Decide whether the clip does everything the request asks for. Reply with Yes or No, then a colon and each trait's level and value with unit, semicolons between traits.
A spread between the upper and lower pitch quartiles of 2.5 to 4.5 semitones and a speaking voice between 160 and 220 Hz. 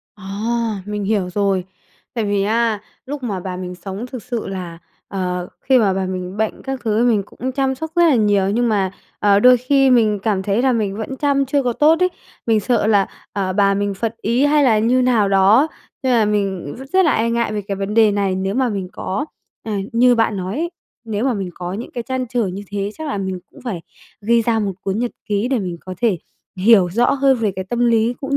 Yes: average, 3.9 semitones; high, 215 Hz